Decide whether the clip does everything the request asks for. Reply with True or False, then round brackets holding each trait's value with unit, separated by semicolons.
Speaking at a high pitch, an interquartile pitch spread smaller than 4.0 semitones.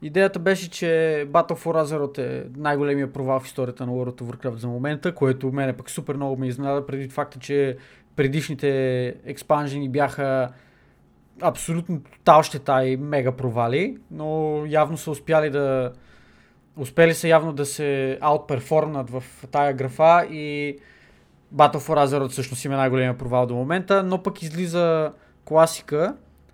False (140 Hz; 3.1 semitones)